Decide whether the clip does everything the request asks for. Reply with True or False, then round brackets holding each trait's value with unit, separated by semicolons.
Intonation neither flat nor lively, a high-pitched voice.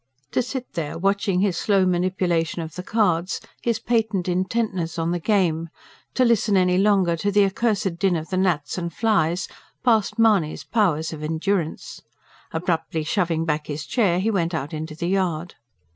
False (3.7 semitones; 180 Hz)